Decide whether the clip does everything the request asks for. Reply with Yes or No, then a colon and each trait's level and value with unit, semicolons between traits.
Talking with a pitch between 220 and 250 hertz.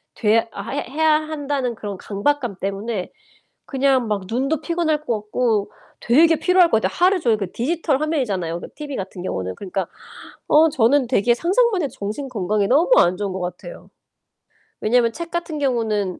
Yes: high, 245 Hz